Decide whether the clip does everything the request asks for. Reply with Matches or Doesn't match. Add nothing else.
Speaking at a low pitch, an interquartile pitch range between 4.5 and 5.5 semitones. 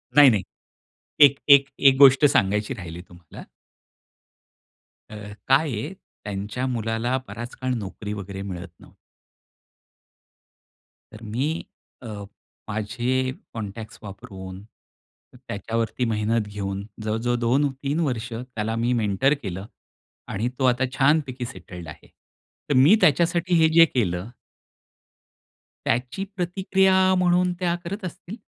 Matches